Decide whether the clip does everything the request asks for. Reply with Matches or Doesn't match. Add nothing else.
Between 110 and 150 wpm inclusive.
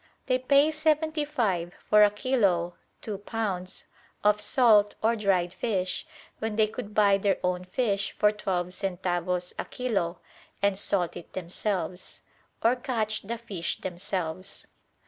Matches